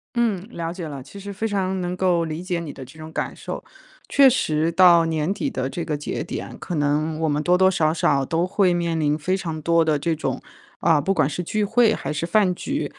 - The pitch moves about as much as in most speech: Yes, average, 3.3 semitones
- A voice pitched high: No, medium, 170 Hz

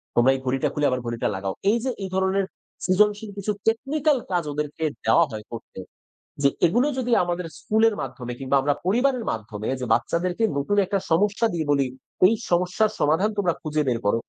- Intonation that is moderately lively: No, wide, 7.7 semitones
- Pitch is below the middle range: No, medium, 175 Hz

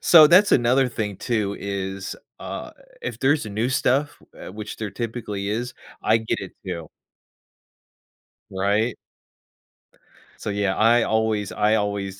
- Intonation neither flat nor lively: Yes, average, 3.3 semitones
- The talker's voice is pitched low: Yes, low, 110 Hz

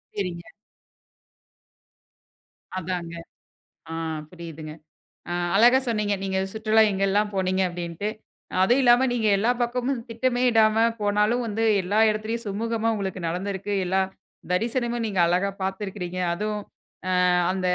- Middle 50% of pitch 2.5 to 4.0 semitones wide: Yes, average, 3.4 semitones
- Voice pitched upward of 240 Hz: No, high, 205 Hz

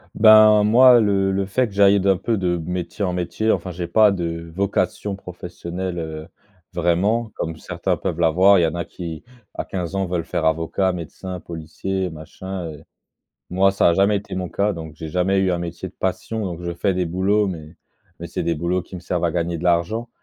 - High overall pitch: No, very low, 90 Hz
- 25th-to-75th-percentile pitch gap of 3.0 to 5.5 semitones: No, narrow, 2.4 semitones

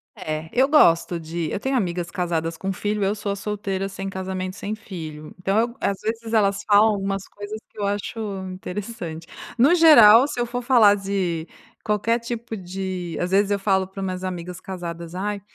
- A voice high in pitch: Yes, high, 195 Hz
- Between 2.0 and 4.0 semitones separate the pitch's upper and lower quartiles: Yes, average, 2.9 semitones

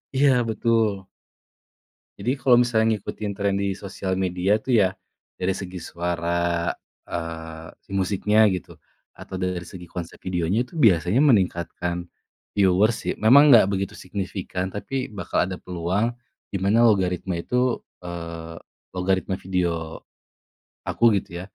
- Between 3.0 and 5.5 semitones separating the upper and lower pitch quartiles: Yes, average, 3.5 semitones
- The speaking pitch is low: Yes, very low, 95 Hz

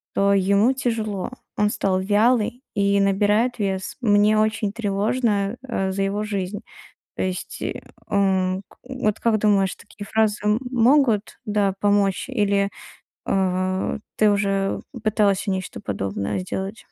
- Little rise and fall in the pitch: Yes, narrow, 1.9 semitones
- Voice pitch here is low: No, high, 205 Hz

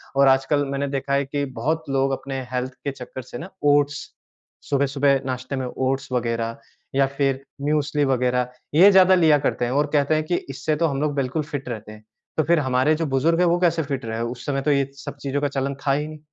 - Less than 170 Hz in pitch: Yes, medium, 140 Hz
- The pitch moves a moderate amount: No, narrow, 2.2 semitones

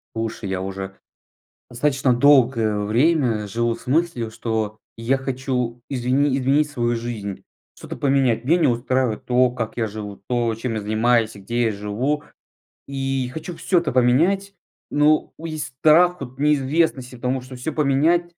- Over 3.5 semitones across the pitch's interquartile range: Yes, average, 4.1 semitones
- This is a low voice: Yes, low, 125 Hz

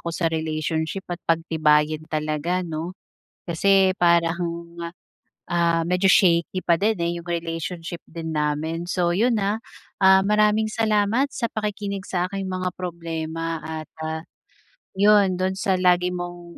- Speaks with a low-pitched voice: No, medium, 175 Hz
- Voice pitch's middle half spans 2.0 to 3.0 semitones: Yes, average, 2.7 semitones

